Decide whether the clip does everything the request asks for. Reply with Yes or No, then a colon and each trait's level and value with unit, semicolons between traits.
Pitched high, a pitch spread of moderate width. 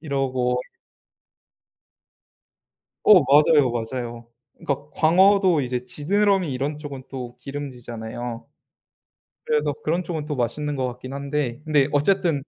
No: medium, 140 Hz; average, 3.5 semitones